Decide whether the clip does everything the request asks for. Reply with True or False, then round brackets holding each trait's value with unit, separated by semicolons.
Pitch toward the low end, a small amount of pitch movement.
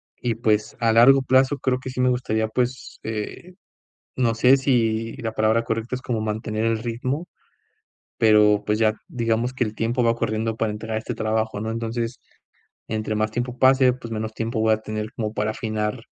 True (115 Hz; 2.1 semitones)